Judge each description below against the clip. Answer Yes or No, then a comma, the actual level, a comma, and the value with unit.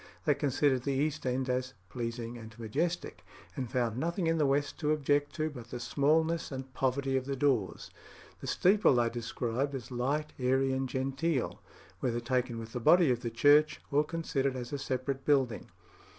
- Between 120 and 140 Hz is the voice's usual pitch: Yes, low, 135 Hz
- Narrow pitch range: No, average, 3.0 semitones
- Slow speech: No, average, 180 wpm